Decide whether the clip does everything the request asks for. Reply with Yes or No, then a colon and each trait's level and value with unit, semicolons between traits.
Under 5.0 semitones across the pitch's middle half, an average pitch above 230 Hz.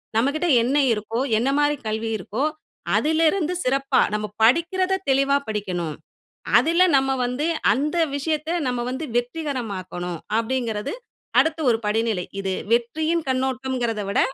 No: average, 5.3 semitones; very high, 255 Hz